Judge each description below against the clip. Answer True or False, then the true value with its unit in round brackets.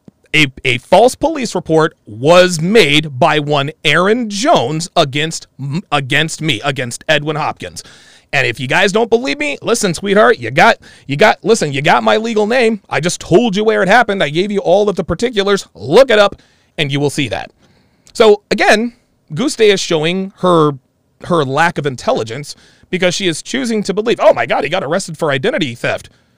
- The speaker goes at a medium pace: True (190 wpm)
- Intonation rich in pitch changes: True (6.0 semitones)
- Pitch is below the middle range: False (175 Hz)